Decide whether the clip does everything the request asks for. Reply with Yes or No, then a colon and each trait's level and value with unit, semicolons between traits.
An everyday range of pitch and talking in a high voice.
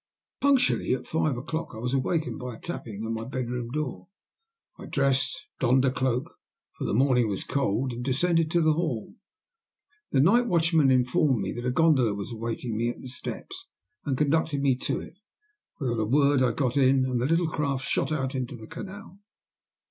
No: average, 4.2 semitones; low, 130 Hz